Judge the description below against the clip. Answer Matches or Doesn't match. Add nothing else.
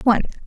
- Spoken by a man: Doesn't match